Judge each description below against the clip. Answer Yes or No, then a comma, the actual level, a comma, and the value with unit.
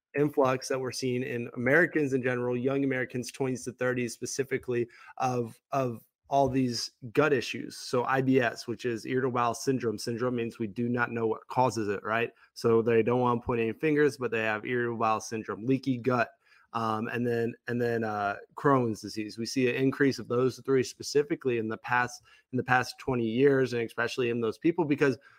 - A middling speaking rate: Yes, average, 195 wpm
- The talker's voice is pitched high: No, low, 125 Hz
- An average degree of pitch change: No, narrow, 2.3 semitones